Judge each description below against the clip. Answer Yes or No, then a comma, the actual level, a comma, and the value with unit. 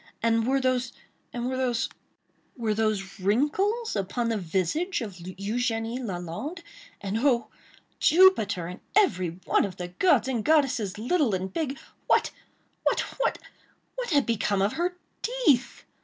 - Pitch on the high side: Yes, high, 230 Hz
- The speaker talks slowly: Yes, slow, 120 wpm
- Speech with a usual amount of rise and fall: No, wide, 6.4 semitones